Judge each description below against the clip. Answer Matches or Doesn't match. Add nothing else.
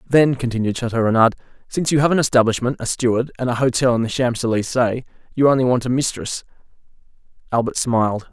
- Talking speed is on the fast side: Doesn't match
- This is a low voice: Matches